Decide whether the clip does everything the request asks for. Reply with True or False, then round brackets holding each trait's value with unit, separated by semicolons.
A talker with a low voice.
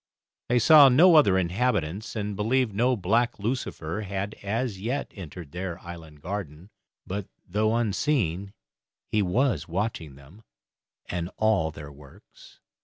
True (100 Hz)